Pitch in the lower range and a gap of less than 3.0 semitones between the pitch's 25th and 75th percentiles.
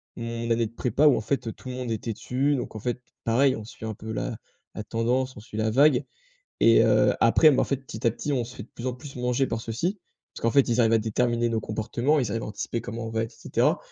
Yes: low, 115 Hz; narrow, 2.5 semitones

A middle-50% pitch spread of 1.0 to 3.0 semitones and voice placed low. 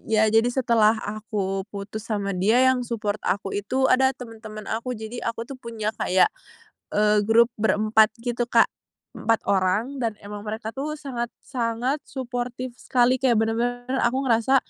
No: narrow, 2.5 semitones; high, 230 Hz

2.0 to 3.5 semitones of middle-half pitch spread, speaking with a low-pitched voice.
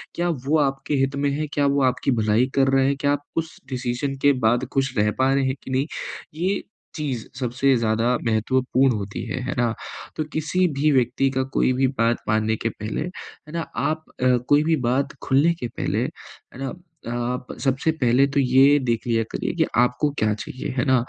Yes: average, 2.8 semitones; low, 130 Hz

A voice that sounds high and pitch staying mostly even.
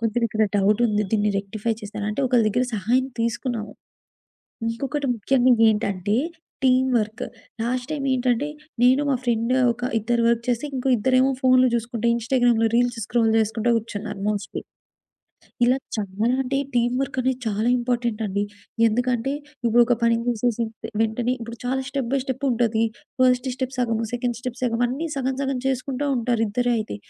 Yes: high, 240 Hz; narrow, 2.3 semitones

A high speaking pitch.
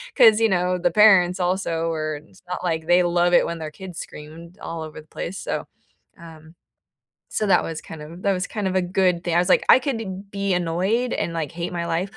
No: medium, 175 Hz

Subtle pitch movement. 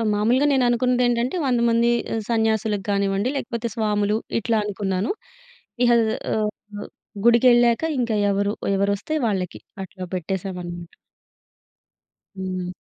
No: average, 3.4 semitones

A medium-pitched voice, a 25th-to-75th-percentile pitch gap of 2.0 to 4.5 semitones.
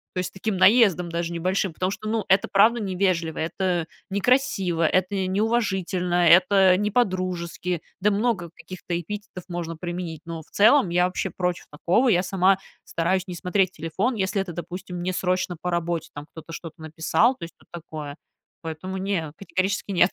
Yes: medium, 180 Hz; narrow, 2.4 semitones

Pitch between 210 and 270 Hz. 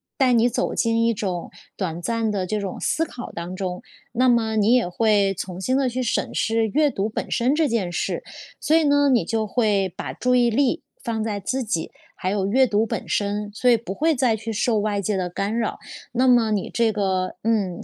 Yes: high, 220 Hz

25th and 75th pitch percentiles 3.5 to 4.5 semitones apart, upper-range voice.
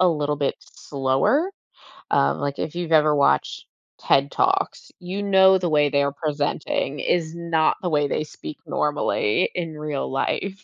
No: average, 3.8 semitones; medium, 155 Hz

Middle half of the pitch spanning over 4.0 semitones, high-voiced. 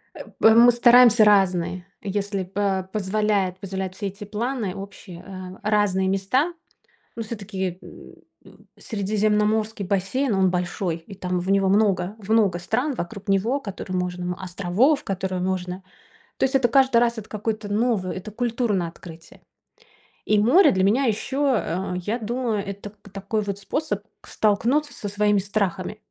No: average, 2.9 semitones; high, 200 Hz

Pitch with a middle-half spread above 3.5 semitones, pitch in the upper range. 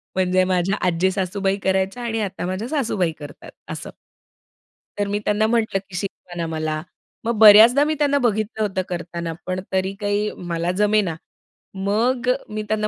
No: average, 2.9 semitones; high, 200 Hz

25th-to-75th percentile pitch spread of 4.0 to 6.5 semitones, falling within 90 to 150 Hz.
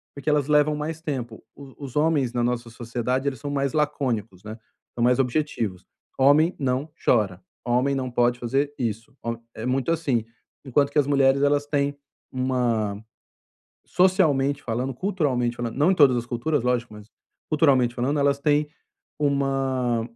No: average, 3.2 semitones; low, 135 Hz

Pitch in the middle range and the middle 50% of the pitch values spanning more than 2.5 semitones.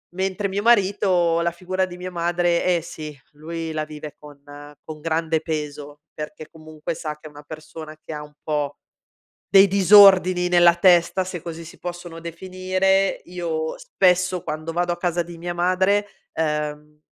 Yes: medium, 170 Hz; average, 2.9 semitones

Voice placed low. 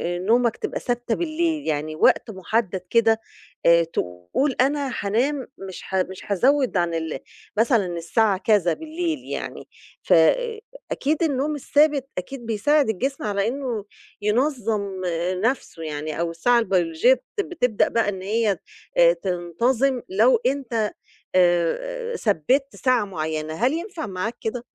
No: high, 225 Hz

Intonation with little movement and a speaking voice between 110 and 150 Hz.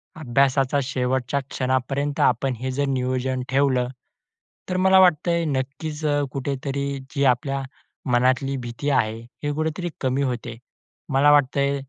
Yes: narrow, 2.1 semitones; low, 135 Hz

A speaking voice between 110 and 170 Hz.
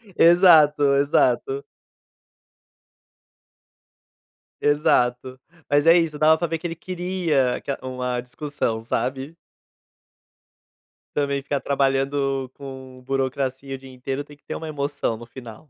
Yes: medium, 140 Hz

